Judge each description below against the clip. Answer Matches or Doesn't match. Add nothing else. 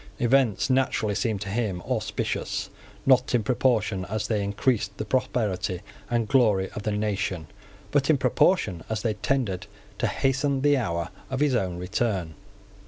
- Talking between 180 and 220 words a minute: Doesn't match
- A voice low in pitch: Matches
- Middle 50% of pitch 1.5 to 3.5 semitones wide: Doesn't match